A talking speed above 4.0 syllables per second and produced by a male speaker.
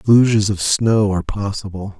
Yes: 5.2 syllables/s; male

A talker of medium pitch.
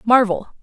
No: high, 225 Hz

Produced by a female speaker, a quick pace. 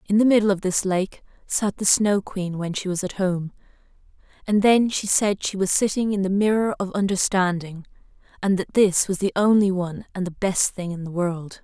Yes: female; fast, 210 wpm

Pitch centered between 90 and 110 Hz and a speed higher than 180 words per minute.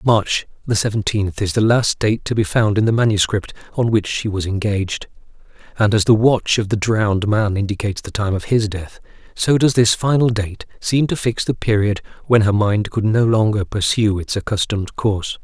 Yes: low, 105 Hz; average, 200 wpm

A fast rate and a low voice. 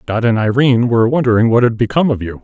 Yes: fast, 245 wpm; low, 120 Hz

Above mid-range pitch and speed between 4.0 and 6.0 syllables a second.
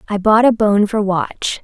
Yes: high, 210 Hz; 4.1 syllables/s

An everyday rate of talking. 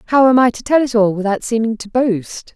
No: fast, 260 wpm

